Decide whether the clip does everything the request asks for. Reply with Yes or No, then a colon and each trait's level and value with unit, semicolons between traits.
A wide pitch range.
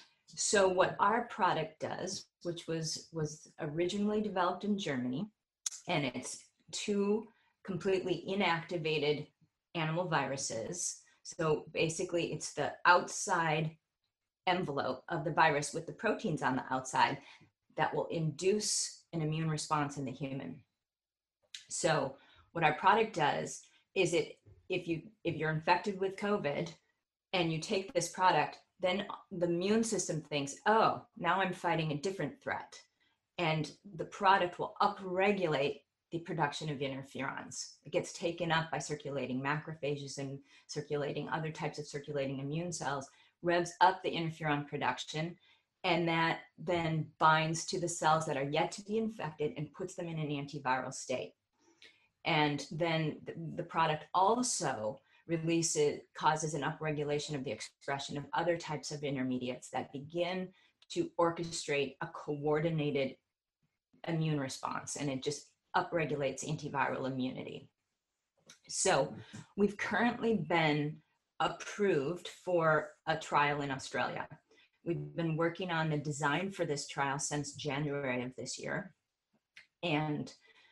No: average, 3.5 semitones